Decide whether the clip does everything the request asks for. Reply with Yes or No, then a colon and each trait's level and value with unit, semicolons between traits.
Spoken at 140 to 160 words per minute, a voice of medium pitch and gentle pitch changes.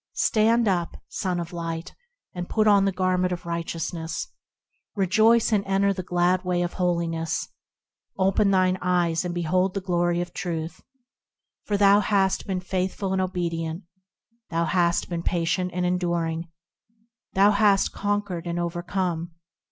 Yes: average, 145 wpm; medium, 180 Hz; narrow, 2.3 semitones